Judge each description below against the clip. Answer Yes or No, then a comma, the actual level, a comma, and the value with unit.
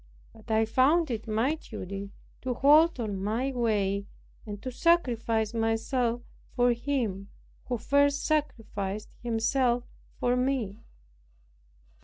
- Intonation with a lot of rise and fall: No, average, 3.6 semitones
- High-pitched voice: Yes, high, 235 Hz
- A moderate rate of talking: No, slow, 115 wpm